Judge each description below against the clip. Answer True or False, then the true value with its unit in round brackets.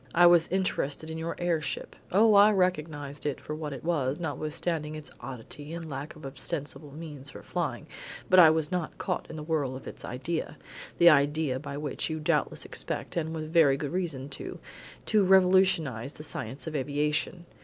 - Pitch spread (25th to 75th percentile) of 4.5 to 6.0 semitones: False (3.1 semitones)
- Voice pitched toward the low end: False (155 Hz)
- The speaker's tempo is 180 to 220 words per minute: True (185 wpm)